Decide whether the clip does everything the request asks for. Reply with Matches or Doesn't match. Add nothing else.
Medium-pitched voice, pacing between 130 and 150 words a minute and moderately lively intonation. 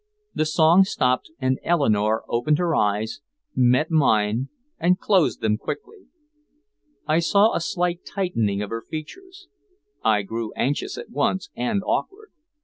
Doesn't match